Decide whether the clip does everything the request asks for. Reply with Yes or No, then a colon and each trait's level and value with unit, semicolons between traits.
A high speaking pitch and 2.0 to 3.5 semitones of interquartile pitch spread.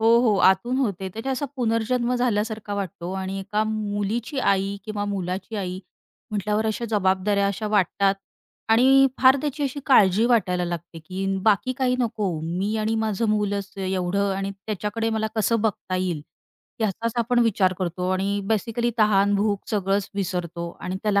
Yes: high, 205 Hz; average, 2.8 semitones